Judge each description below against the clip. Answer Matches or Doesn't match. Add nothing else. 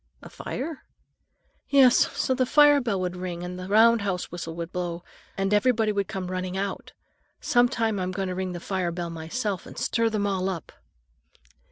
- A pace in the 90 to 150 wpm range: Doesn't match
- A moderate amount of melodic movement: Matches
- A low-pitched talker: Doesn't match